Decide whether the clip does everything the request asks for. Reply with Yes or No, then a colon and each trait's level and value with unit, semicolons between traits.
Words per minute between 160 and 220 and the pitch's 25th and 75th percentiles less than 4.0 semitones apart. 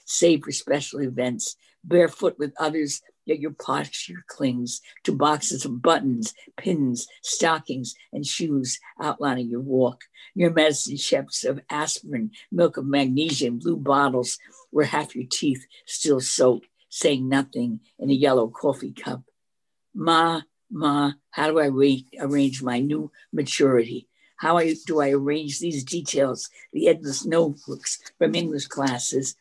No: average, 140 wpm; average, 3.2 semitones